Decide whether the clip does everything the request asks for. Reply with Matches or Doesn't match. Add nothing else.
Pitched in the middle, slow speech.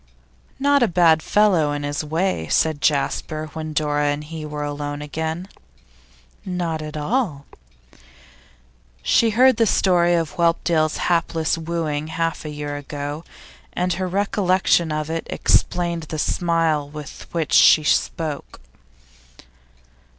Matches